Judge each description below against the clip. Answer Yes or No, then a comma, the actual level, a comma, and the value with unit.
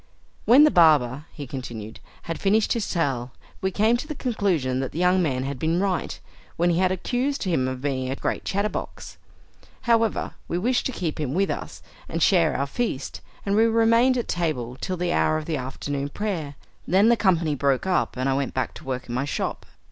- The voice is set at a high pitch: No, medium, 170 Hz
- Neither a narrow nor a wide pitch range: No, wide, 6.9 semitones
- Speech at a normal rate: No, fast, 210 wpm